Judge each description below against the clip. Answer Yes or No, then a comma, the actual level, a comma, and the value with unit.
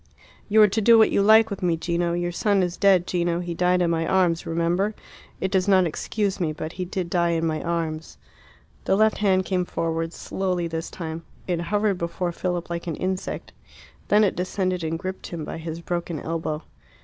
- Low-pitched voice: No, medium, 175 Hz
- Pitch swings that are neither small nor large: No, narrow, 2.3 semitones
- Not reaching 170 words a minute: No, fast, 205 wpm